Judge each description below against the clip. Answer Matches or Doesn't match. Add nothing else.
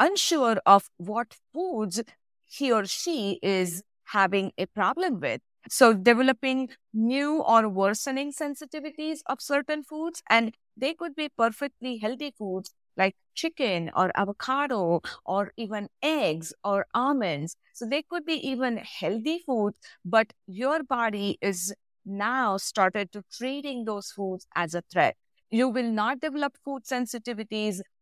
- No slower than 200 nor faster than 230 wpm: Doesn't match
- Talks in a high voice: Matches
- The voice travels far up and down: Matches